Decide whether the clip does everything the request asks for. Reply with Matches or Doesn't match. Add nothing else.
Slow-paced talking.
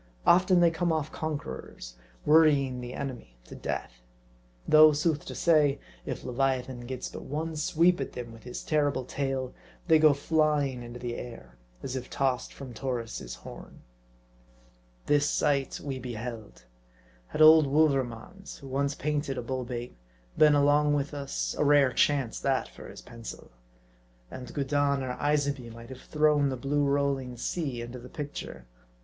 Doesn't match